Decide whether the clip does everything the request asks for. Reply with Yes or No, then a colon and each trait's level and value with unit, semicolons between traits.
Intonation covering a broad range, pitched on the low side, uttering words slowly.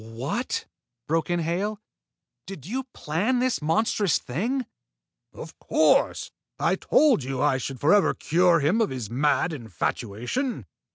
No: wide, 8.5 semitones; medium, 165 Hz; slow, 130 wpm